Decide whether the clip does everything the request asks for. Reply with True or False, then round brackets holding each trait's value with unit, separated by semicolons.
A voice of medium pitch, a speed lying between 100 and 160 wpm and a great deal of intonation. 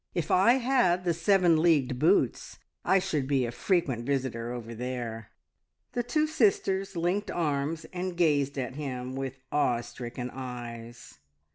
True (145 Hz; 145 wpm; 6.2 semitones)